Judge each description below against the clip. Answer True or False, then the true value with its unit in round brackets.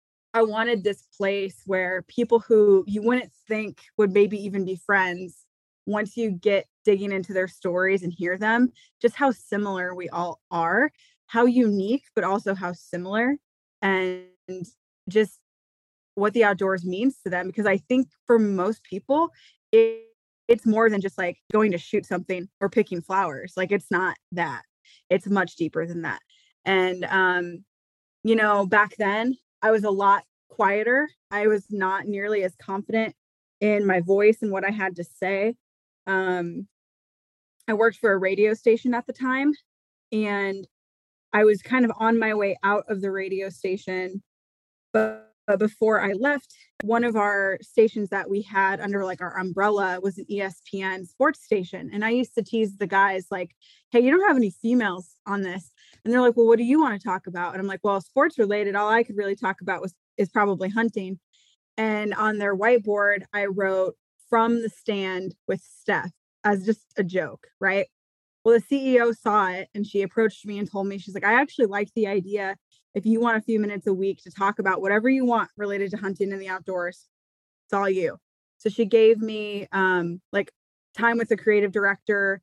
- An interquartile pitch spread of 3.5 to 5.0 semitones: False (2.8 semitones)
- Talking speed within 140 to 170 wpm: False (185 wpm)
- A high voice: True (200 Hz)